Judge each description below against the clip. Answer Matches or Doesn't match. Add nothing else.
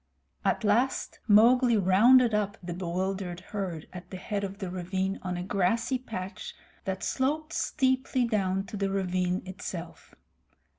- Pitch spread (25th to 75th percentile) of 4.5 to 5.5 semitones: Doesn't match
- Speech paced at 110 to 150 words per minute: Matches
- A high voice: Matches